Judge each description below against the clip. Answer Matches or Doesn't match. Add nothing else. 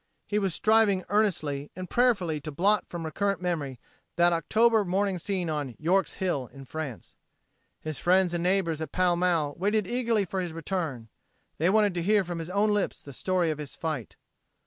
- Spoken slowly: Doesn't match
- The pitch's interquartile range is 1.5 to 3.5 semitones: Doesn't match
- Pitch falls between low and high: Matches